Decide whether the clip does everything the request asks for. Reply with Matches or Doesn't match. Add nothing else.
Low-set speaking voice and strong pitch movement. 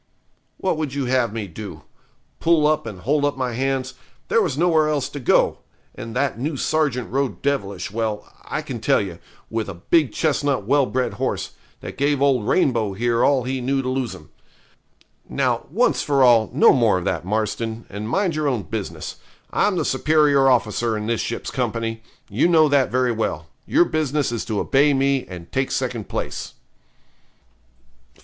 Doesn't match